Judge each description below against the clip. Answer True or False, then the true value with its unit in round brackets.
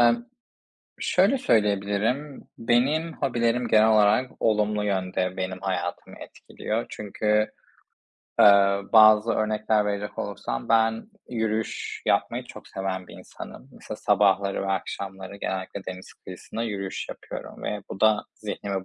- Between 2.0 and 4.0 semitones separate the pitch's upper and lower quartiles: True (2.5 semitones)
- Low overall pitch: True (105 Hz)